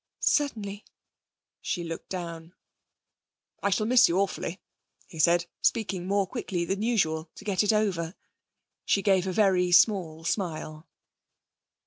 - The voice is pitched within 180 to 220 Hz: Yes, medium, 185 Hz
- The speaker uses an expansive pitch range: No, average, 3.3 semitones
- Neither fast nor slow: No, slow, 130 wpm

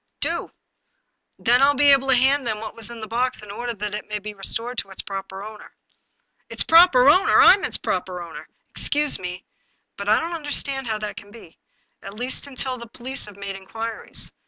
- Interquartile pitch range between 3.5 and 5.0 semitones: Yes, average, 4.7 semitones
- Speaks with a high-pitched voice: Yes, high, 230 Hz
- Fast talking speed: Yes, fast, 230 wpm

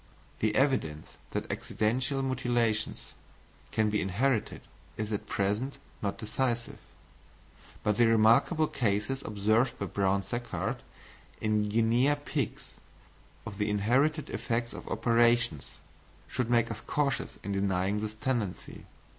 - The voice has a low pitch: Yes, low, 115 Hz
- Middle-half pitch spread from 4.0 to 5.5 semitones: No, average, 3.2 semitones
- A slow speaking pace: Yes, slow, 120 wpm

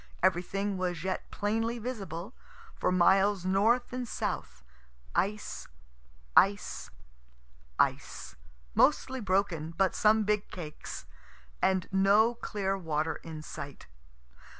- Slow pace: Yes, slow, 105 wpm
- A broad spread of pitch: No, average, 3.2 semitones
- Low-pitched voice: No, high, 195 Hz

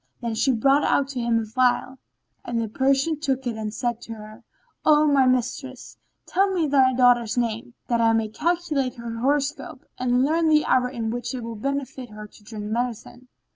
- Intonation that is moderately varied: Yes, average, 3.2 semitones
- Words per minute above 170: Yes, average, 195 wpm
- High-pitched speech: Yes, very high, 250 Hz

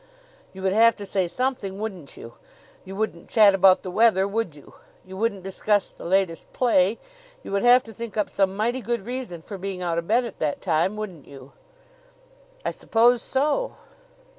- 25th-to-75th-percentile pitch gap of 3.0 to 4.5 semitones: Yes, average, 3.7 semitones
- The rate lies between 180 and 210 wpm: Yes, average, 190 wpm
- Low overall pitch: No, high, 200 Hz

